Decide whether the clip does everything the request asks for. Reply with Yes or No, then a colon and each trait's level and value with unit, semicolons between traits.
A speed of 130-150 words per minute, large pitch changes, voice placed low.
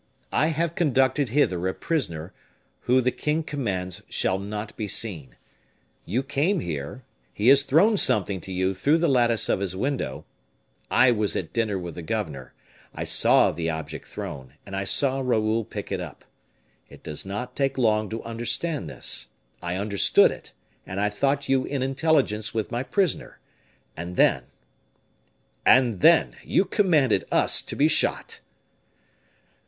No: average, 160 wpm; wide, 6.6 semitones; low, 115 Hz